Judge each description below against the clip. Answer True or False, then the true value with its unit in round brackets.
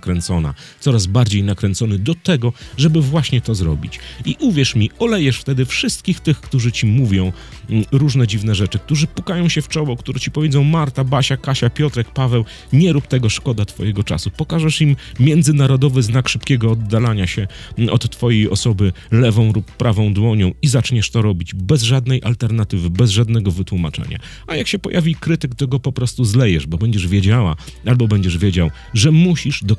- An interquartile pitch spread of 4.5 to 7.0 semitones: True (5.1 semitones)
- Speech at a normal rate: False (170 wpm)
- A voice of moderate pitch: False (120 Hz)